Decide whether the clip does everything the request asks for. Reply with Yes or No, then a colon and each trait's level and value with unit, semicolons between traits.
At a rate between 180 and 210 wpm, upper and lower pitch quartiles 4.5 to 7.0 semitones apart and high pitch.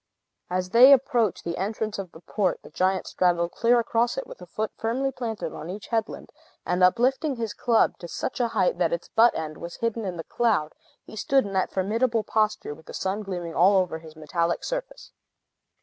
Yes: fast, 205 wpm; average, 4.8 semitones; high, 210 Hz